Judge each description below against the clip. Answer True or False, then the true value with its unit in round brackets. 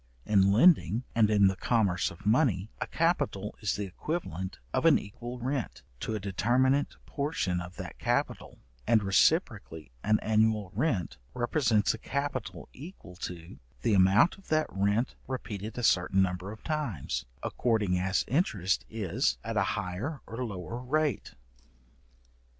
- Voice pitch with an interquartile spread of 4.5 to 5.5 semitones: True (4.9 semitones)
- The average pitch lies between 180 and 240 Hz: False (110 Hz)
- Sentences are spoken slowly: False (145 wpm)